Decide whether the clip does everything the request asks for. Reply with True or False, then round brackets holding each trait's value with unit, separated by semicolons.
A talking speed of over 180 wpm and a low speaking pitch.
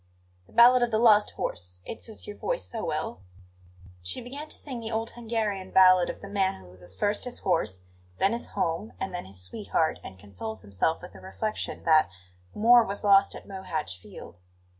False (195 wpm; 195 Hz)